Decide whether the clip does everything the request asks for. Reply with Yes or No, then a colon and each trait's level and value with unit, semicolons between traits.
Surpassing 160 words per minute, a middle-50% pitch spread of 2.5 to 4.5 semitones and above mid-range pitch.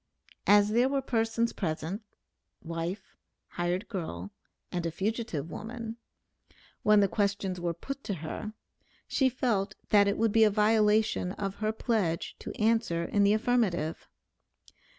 No: average, 140 wpm; average, 4.1 semitones; high, 205 Hz